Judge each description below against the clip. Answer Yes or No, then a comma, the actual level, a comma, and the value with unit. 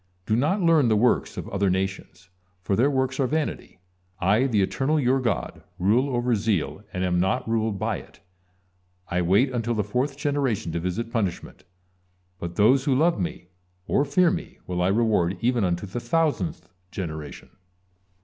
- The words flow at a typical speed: Yes, average, 170 wpm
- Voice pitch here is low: Yes, low, 110 Hz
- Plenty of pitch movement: Yes, wide, 6.0 semitones